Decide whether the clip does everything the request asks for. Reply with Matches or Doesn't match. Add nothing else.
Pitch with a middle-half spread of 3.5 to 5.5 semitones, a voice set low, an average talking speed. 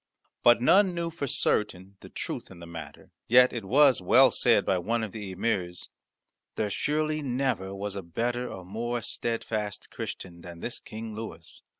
Matches